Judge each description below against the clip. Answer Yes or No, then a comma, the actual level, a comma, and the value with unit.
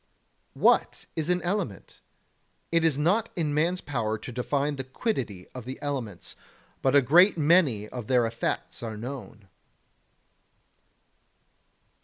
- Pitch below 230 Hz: Yes, medium, 140 Hz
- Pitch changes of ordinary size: No, wide, 6.2 semitones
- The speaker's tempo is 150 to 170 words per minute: No, slow, 135 wpm